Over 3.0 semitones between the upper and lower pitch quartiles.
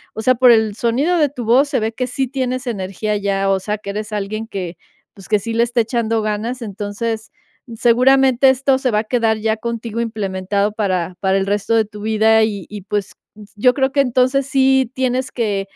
Yes: average, 3.5 semitones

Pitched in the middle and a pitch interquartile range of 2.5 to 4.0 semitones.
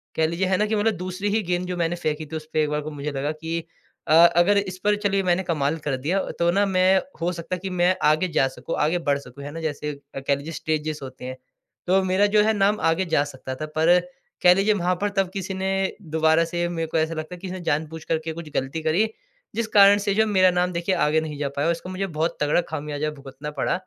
Yes: medium, 165 Hz; average, 3.5 semitones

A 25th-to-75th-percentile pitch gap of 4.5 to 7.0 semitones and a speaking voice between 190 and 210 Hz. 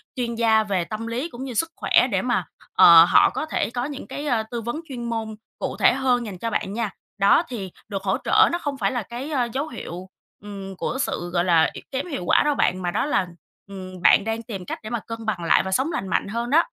No: average, 4.9 semitones; high, 230 Hz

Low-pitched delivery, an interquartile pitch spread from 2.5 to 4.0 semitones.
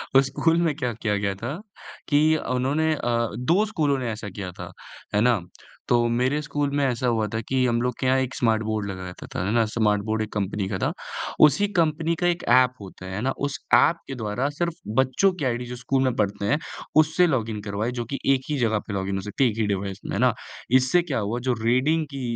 No: low, 125 Hz; average, 4.9 semitones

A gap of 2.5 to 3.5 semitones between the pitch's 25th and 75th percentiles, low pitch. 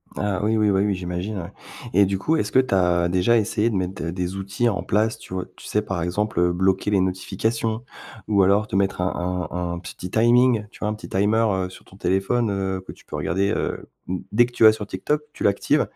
Yes: average, 2.8 semitones; low, 100 Hz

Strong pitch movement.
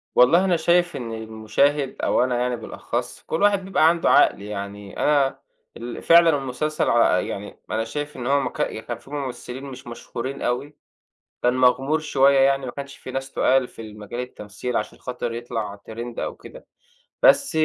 No: average, 3.7 semitones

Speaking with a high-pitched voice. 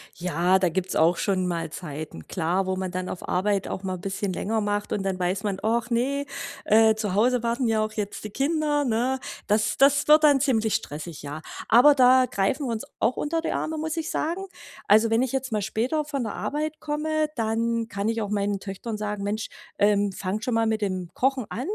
Yes: high, 220 Hz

